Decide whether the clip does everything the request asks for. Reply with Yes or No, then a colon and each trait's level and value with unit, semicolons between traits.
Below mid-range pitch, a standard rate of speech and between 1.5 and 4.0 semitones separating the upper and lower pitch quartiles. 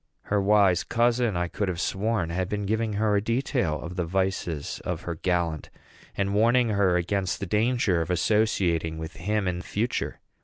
Yes: low, 100 Hz; average, 180 wpm; average, 3.7 semitones